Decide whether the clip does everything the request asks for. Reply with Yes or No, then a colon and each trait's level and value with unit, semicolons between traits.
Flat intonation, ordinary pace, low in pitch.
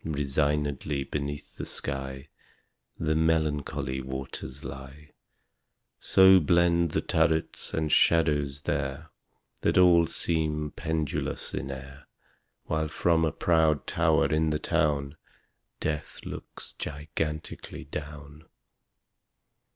No: narrow, 2.2 semitones; slow, 100 wpm; very low, 75 Hz